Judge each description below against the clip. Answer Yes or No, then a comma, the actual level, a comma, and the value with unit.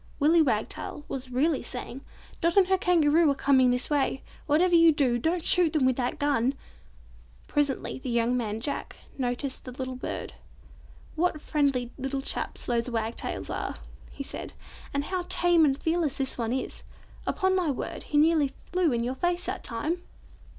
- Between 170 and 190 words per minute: Yes, average, 175 wpm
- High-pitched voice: Yes, very high, 280 Hz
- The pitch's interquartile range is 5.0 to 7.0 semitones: No, average, 4.4 semitones